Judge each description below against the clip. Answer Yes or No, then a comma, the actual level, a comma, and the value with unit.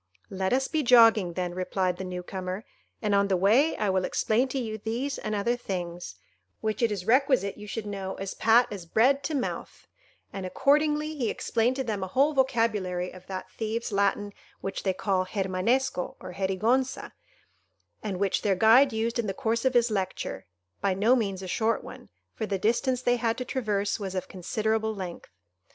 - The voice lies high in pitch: Yes, high, 215 Hz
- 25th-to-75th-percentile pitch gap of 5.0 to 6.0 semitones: No, average, 4.2 semitones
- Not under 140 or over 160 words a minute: No, average, 190 wpm